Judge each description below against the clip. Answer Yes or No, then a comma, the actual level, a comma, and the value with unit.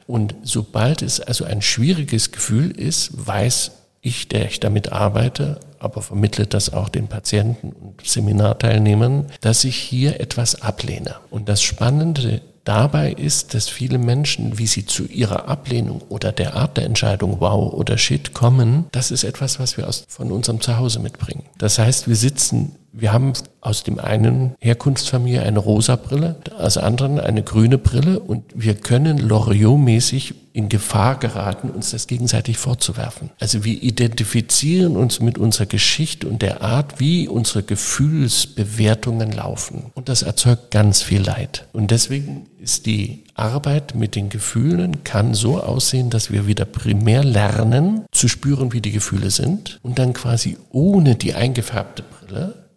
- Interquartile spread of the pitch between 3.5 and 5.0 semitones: Yes, average, 3.9 semitones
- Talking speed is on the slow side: No, average, 155 wpm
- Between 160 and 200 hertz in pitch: No, low, 120 Hz